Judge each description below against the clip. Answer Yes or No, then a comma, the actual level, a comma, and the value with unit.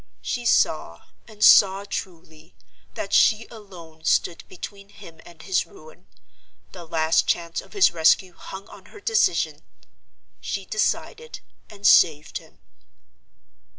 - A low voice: No, high, 190 Hz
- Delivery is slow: Yes, slow, 125 wpm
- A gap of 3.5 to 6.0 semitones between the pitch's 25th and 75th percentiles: Yes, average, 4.3 semitones